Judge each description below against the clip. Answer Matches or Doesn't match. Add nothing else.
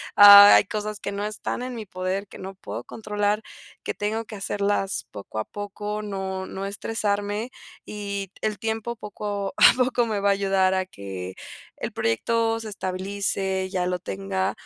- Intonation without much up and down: Matches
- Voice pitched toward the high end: Matches